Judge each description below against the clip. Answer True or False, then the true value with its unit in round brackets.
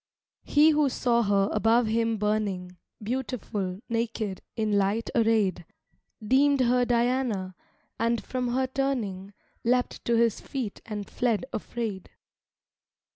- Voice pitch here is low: False (230 Hz)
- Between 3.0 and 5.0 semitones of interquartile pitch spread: True (3.3 semitones)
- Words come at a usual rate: False (120 wpm)